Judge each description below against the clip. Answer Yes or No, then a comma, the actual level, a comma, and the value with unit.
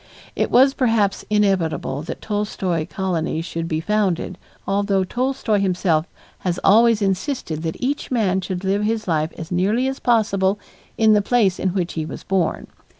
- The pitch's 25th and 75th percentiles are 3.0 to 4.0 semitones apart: Yes, average, 3.7 semitones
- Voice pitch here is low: No, high, 195 Hz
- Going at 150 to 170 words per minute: Yes, average, 160 wpm